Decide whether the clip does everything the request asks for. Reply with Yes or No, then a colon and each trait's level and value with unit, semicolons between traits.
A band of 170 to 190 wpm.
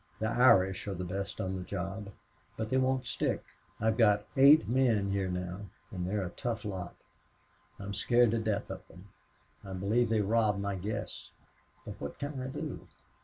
Yes: average, 185 wpm